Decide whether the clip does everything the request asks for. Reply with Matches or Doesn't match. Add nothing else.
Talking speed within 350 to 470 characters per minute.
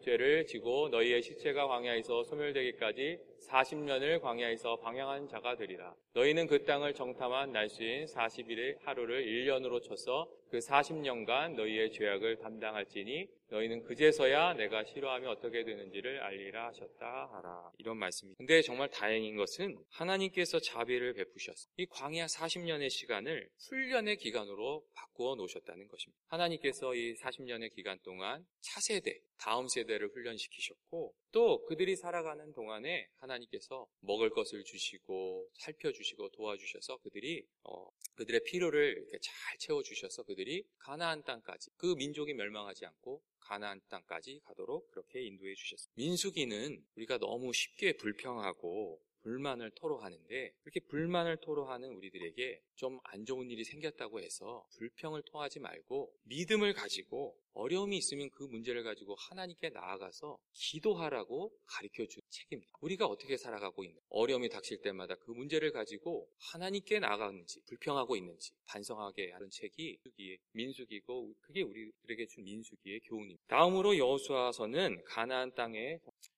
Matches